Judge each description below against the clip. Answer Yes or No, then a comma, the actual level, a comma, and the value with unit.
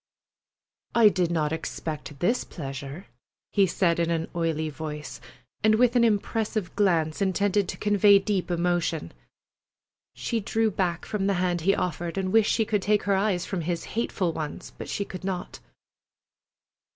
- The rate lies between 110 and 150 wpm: No, average, 160 wpm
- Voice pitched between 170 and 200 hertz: Yes, medium, 185 Hz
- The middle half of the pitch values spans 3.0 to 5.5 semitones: Yes, average, 3.8 semitones